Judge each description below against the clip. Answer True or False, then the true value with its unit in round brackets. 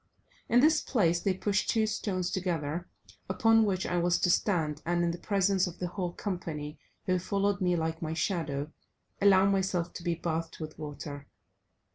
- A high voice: False (180 Hz)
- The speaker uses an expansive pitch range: False (3.3 semitones)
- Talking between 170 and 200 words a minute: True (175 wpm)